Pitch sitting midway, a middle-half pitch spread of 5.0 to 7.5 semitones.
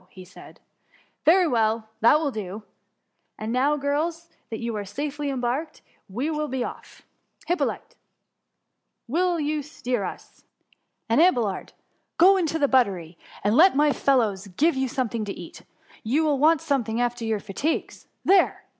No: very high, 265 Hz; wide, 5.5 semitones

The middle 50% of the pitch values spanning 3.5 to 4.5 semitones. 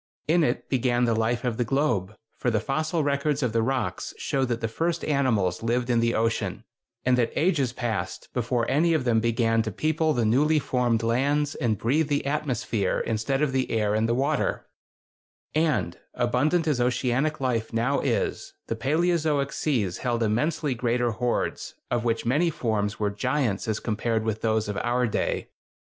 Yes: average, 4.0 semitones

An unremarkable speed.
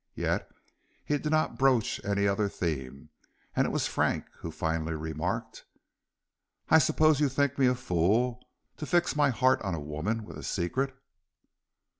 Yes: average, 160 wpm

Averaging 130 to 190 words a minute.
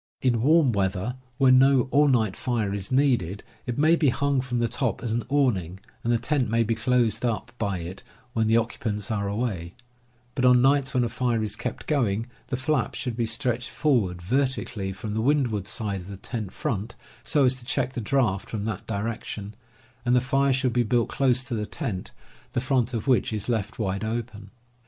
No: fast, 205 wpm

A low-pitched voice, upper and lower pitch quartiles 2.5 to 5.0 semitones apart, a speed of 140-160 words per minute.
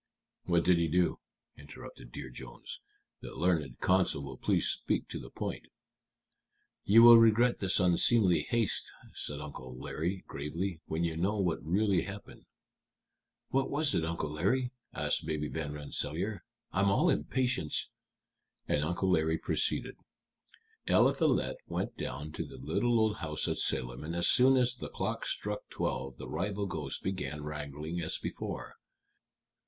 No: very low, 85 Hz; wide, 5.4 semitones; average, 150 wpm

